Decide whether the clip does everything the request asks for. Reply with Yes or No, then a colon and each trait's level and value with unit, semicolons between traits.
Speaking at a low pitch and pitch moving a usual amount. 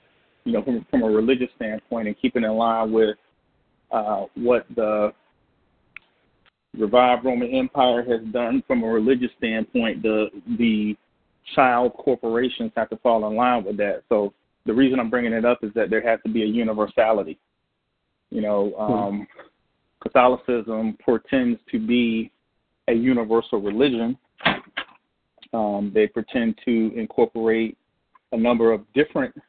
No: low, 115 Hz; narrow, 2.2 semitones